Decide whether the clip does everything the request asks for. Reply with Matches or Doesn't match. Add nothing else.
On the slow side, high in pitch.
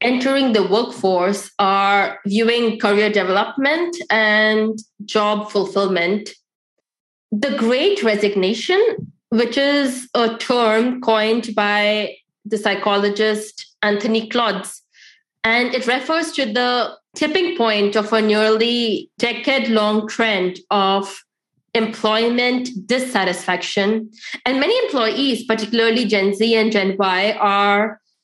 Matches